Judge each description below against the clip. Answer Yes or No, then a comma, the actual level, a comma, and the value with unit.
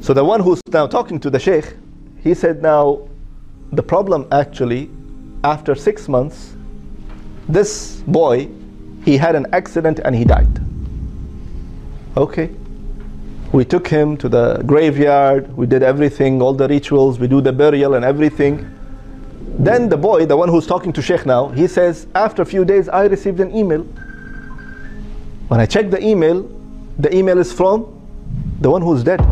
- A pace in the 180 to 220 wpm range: No, average, 160 wpm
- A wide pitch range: Yes, wide, 6.2 semitones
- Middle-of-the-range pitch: Yes, medium, 145 Hz